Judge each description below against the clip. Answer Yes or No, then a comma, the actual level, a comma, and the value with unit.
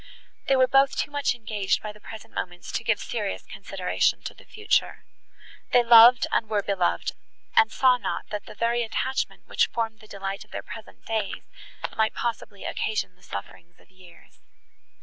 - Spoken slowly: No, average, 175 wpm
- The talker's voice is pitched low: No, high, 220 Hz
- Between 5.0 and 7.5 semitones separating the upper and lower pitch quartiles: No, average, 3.4 semitones